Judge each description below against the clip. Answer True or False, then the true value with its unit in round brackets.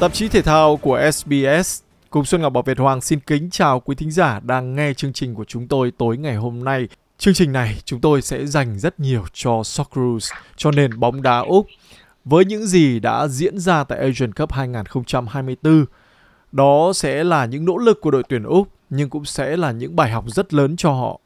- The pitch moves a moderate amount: True (3.8 semitones)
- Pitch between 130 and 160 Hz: True (140 Hz)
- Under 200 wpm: False (215 wpm)